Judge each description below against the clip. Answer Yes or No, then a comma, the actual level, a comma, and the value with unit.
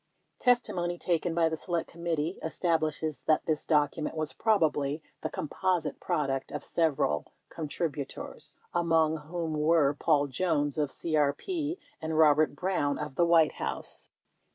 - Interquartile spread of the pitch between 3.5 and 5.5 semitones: No, narrow, 2.5 semitones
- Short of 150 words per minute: Yes, slow, 135 wpm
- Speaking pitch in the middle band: Yes, medium, 160 Hz